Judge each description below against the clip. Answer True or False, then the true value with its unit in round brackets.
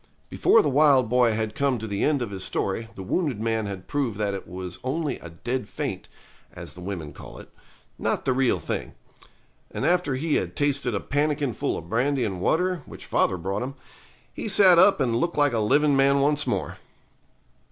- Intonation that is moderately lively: False (5.7 semitones)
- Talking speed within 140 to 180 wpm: False (205 wpm)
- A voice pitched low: True (130 Hz)